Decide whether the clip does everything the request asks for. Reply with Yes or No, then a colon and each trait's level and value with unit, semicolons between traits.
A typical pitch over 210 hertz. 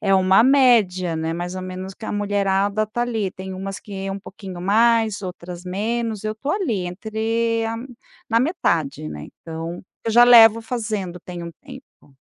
No: high, 200 Hz